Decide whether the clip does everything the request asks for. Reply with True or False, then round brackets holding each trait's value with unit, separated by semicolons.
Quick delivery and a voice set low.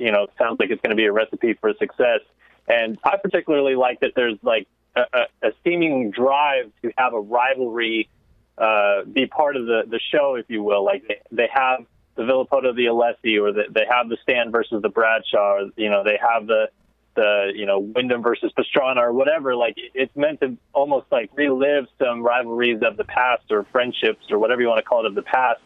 True (220 wpm; 125 Hz)